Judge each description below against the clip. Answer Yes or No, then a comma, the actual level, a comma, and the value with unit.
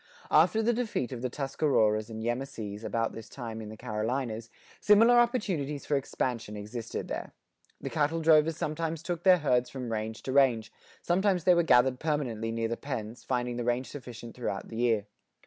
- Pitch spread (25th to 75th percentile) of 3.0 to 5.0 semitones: No, wide, 5.4 semitones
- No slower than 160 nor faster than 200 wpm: Yes, average, 180 wpm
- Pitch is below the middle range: Yes, low, 125 Hz